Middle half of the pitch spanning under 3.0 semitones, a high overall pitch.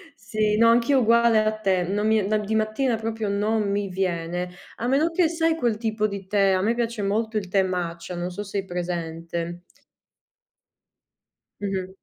No: average, 3.4 semitones; high, 210 Hz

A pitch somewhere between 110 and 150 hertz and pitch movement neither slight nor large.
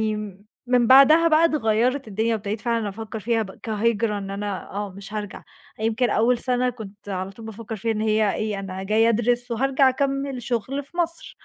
No: high, 225 Hz; average, 3.3 semitones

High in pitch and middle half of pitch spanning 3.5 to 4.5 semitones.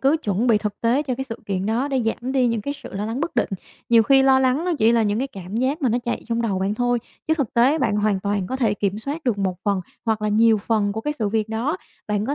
Yes: high, 230 Hz; average, 4.0 semitones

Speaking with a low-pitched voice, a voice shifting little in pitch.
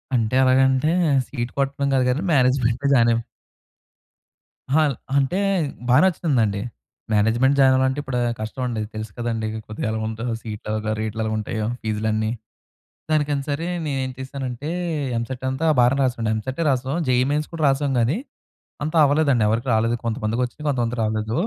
No: low, 125 Hz; average, 3.5 semitones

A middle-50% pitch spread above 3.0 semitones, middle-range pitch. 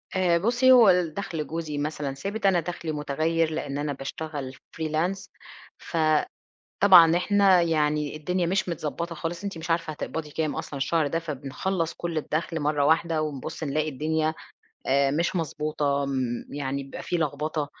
No: narrow, 2.6 semitones; medium, 160 Hz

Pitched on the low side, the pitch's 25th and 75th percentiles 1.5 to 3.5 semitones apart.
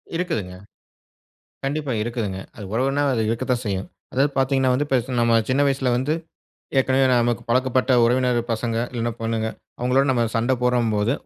Yes: low, 125 Hz; narrow, 2.5 semitones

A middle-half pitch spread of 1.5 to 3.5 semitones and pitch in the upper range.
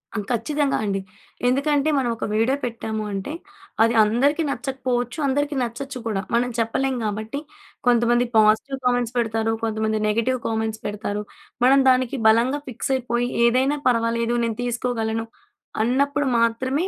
Yes: average, 3.0 semitones; high, 240 Hz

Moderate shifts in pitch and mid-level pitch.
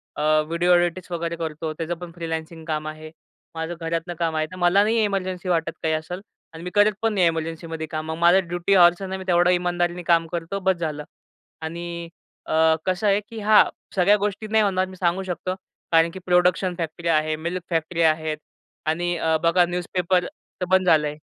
No: narrow, 2.2 semitones; medium, 175 Hz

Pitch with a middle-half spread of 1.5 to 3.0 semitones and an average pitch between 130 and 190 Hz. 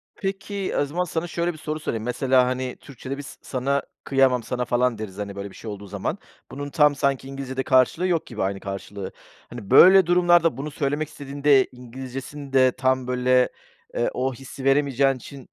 Yes: average, 2.7 semitones; low, 135 Hz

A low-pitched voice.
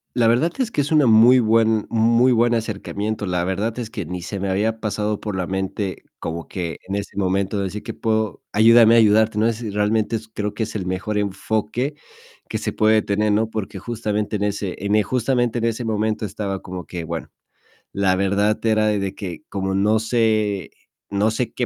Yes: low, 105 Hz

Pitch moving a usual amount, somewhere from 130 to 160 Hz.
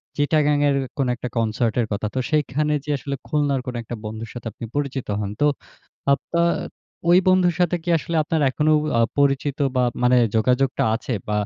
Yes: average, 3.7 semitones; medium, 140 Hz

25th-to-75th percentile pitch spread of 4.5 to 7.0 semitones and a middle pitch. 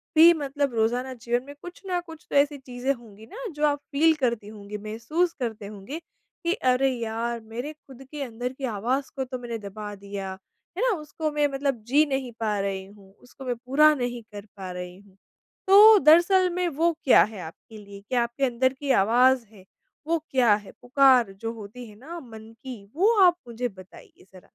No: average, 5.0 semitones; very high, 250 Hz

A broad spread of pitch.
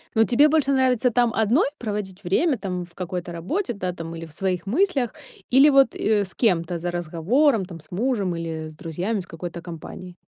Yes: wide, 6.0 semitones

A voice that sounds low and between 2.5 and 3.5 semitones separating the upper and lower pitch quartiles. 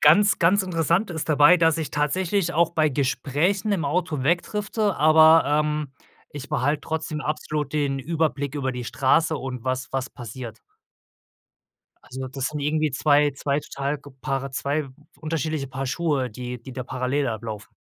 No: medium, 145 Hz; average, 3.2 semitones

